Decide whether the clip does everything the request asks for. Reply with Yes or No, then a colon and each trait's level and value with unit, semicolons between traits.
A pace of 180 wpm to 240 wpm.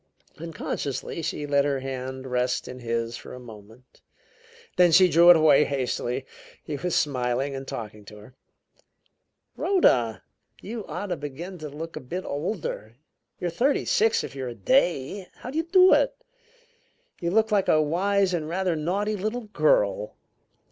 No: average, 160 wpm